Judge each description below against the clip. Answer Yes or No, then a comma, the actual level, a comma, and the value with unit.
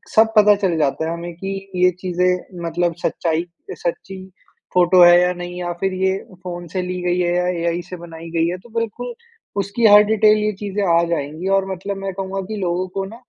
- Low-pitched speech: No, medium, 180 Hz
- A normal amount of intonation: No, narrow, 2.1 semitones